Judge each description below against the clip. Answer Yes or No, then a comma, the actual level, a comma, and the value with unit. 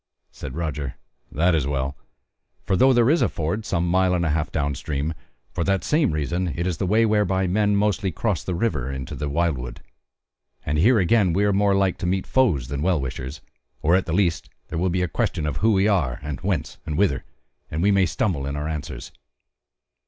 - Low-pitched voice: Yes, very low, 85 Hz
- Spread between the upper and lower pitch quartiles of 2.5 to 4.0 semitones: No, average, 4.9 semitones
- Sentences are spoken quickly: Yes, fast, 210 wpm